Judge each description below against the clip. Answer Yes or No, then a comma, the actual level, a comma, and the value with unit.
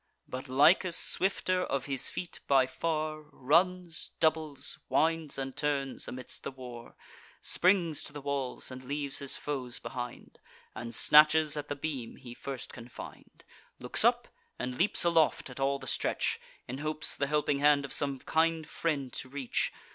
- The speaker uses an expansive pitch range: No, average, 3.2 semitones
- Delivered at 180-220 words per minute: No, average, 160 wpm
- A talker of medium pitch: Yes, medium, 145 Hz